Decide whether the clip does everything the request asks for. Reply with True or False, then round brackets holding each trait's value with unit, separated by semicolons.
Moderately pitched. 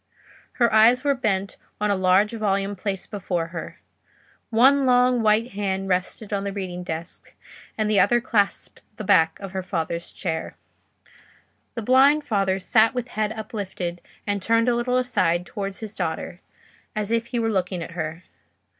False (205 Hz)